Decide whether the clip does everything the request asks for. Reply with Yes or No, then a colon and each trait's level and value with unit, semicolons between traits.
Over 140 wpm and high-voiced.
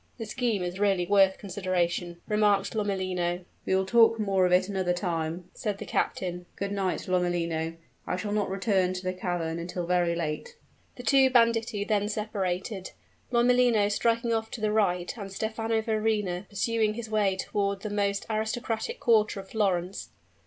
Yes: average, 165 wpm; high, 200 Hz